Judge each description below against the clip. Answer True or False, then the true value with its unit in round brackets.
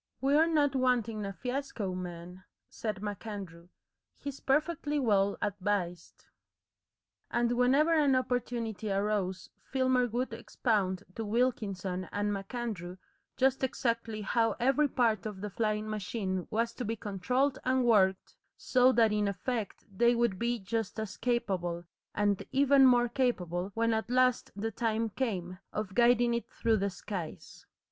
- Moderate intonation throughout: True (4.0 semitones)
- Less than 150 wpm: True (140 wpm)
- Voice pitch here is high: True (225 Hz)